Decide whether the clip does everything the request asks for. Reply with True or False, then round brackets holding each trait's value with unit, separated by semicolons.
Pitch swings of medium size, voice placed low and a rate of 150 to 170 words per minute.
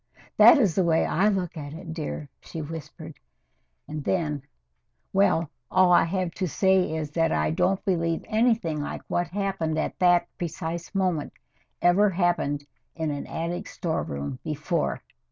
False (3.1 semitones; 170 Hz; 155 wpm)